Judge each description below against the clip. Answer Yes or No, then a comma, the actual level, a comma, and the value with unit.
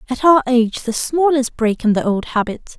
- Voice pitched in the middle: No, very high, 250 Hz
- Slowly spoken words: No, fast, 215 wpm